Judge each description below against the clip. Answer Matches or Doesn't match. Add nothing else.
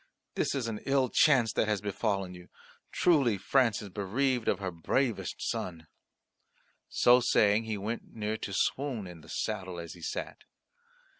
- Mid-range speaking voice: Doesn't match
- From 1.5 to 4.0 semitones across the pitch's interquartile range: Doesn't match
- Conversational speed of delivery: Matches